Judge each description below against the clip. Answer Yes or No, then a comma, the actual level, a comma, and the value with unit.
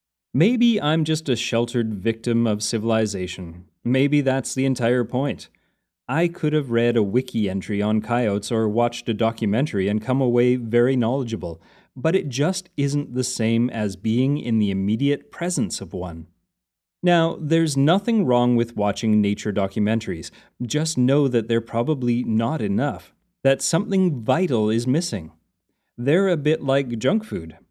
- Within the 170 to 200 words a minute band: No, average, 155 wpm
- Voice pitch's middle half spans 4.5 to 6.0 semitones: Yes, average, 4.9 semitones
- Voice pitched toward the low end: Yes, low, 120 Hz